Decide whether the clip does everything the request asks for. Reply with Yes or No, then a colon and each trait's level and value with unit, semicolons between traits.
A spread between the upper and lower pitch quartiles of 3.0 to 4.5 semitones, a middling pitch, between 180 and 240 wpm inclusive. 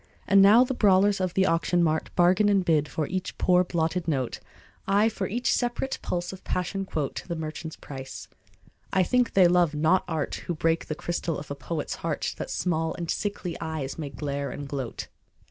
Yes: average, 3.5 semitones; medium, 175 Hz; average, 195 wpm